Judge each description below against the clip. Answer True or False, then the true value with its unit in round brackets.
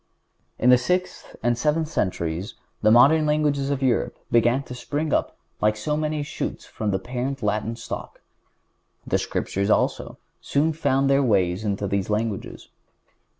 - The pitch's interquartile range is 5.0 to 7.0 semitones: True (5.5 semitones)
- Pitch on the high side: False (125 Hz)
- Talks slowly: False (150 wpm)